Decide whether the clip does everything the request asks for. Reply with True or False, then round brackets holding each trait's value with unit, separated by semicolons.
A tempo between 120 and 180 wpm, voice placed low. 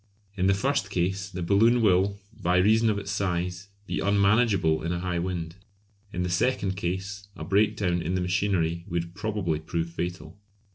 True (175 wpm; 95 Hz)